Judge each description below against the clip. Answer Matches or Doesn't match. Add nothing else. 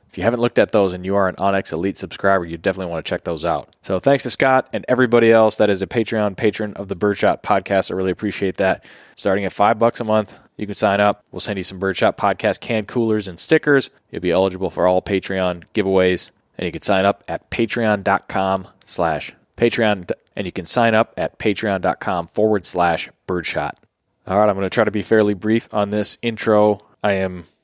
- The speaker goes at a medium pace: Doesn't match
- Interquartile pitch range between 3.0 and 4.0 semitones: Doesn't match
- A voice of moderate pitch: Doesn't match